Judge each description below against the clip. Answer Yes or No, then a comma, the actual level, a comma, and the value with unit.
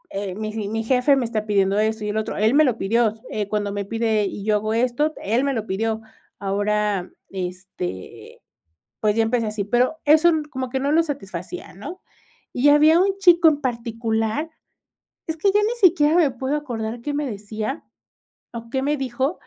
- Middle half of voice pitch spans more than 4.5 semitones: Yes, wide, 5.4 semitones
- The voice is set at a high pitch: Yes, high, 230 Hz